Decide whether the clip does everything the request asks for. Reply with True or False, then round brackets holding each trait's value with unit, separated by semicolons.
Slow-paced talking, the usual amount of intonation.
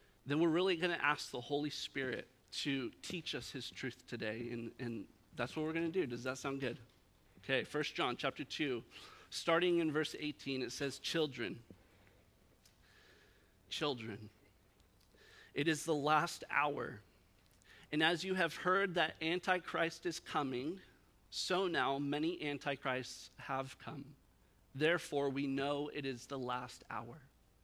False (150 wpm; 4.8 semitones)